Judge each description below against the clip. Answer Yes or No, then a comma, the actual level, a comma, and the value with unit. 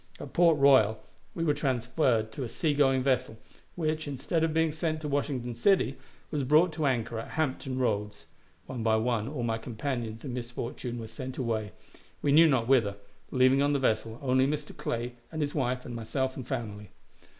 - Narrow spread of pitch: No, average, 3.8 semitones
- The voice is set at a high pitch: No, low, 130 Hz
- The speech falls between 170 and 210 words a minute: Yes, average, 190 wpm